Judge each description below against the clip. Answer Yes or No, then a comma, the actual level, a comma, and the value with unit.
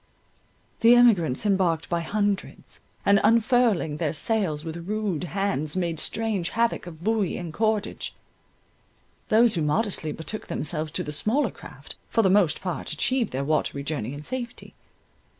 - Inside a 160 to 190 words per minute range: No, average, 150 wpm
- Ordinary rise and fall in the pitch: No, wide, 5.7 semitones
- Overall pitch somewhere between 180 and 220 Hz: Yes, high, 190 Hz